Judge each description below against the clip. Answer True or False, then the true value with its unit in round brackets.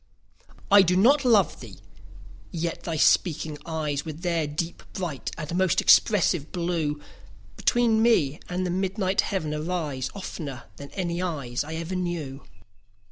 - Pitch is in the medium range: True (170 Hz)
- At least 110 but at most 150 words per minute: True (140 wpm)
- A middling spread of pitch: True (4.0 semitones)